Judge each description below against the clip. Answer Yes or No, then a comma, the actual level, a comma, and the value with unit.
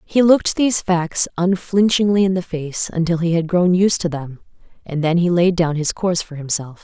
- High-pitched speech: No, medium, 175 Hz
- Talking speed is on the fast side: Yes, fast, 210 wpm